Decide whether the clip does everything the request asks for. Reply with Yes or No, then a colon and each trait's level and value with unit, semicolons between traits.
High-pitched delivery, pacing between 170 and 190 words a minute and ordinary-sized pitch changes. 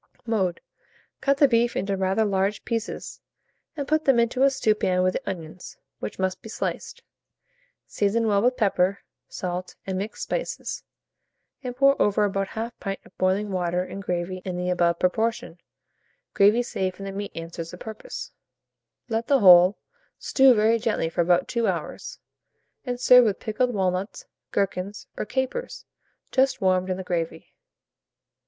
No: high, 200 Hz; average, 160 wpm; average, 4.1 semitones